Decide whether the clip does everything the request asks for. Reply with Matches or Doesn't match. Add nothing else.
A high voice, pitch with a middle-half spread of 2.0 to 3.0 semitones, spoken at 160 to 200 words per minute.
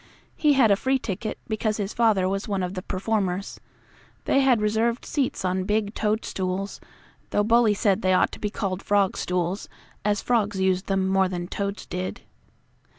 Matches